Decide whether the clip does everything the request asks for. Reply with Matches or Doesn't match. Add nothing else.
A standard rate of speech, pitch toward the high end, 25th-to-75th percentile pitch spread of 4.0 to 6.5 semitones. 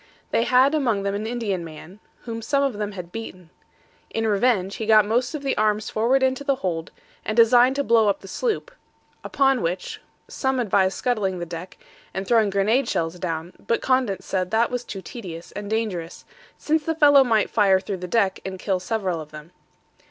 Matches